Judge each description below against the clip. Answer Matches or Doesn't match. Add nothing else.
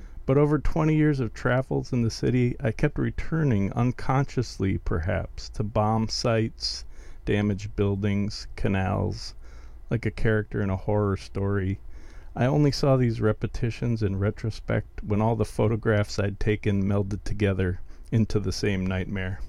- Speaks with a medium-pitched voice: Doesn't match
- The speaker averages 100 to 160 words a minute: Matches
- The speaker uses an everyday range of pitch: Matches